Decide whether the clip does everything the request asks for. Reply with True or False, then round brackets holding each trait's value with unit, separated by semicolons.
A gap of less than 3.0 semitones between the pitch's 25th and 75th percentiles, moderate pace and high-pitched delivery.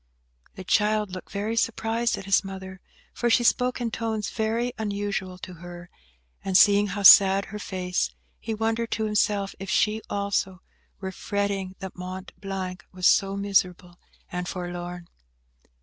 True (2.4 semitones; 150 wpm; 195 Hz)